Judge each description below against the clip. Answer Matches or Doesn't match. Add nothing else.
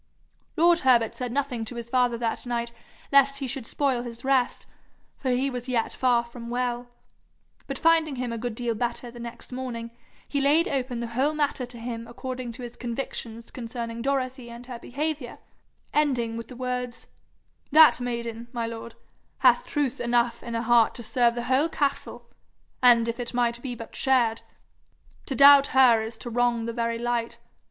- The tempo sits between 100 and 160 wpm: Doesn't match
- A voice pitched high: Matches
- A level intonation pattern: Matches